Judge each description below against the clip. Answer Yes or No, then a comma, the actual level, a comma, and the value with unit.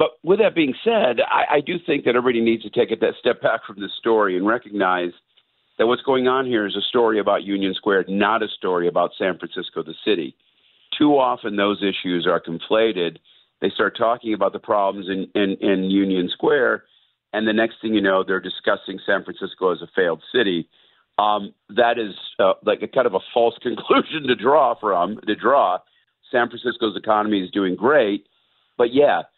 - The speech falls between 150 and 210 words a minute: Yes, average, 195 wpm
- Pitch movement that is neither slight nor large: Yes, average, 3.7 semitones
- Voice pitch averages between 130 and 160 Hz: No, low, 105 Hz